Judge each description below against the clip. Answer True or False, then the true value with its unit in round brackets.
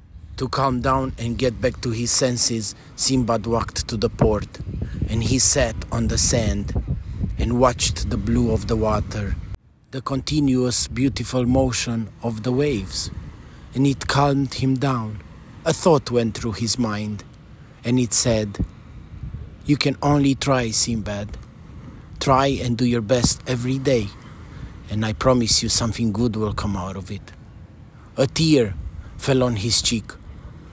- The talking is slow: False (150 wpm)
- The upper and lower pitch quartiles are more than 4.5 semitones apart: False (3.7 semitones)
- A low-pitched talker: True (115 Hz)